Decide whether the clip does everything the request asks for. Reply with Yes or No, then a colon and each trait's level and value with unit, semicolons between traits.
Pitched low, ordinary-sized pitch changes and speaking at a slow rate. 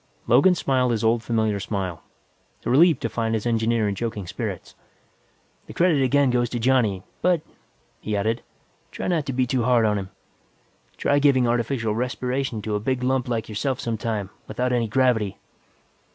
No: low, 120 Hz; average, 3.1 semitones; average, 165 wpm